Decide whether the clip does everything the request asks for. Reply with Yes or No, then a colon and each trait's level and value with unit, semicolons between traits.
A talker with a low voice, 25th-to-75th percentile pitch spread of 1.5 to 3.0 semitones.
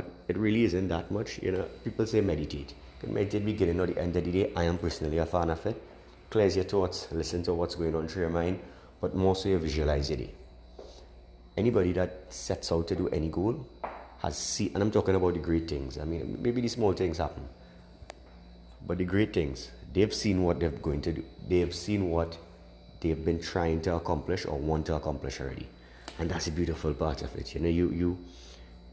No: very low, 85 Hz; average, 3.8 semitones